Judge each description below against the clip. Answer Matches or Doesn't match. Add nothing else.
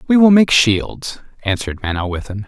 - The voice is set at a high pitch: Doesn't match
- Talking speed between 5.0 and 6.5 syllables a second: Matches